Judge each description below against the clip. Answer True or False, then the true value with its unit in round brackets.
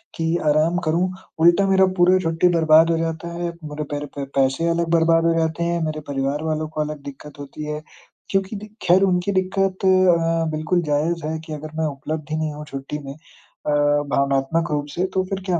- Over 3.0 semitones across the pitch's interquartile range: False (2.5 semitones)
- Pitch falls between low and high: True (160 Hz)